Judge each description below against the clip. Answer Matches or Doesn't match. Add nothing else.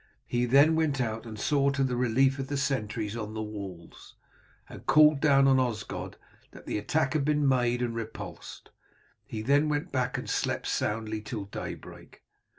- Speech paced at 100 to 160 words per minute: Doesn't match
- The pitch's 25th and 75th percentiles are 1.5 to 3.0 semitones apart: Doesn't match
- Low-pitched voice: Matches